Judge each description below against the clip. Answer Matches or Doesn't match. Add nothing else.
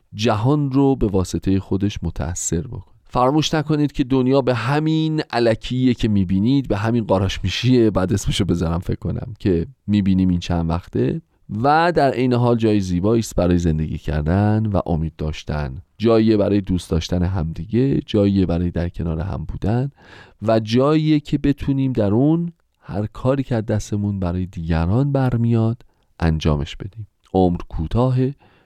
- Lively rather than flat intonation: Matches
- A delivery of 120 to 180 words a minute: Matches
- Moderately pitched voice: Doesn't match